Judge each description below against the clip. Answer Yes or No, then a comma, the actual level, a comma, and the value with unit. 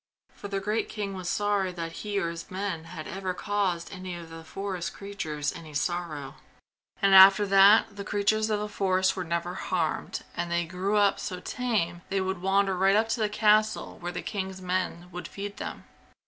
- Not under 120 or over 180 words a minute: No, average, 195 wpm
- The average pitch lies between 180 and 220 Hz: Yes, high, 190 Hz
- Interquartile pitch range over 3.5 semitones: No, average, 2.7 semitones